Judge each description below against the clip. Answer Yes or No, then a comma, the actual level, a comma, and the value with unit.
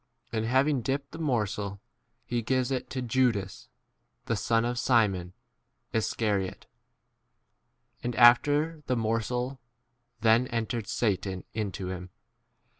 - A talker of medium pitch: No, low, 115 Hz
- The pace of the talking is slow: Yes, slow, 125 wpm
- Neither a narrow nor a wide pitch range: Yes, average, 3.4 semitones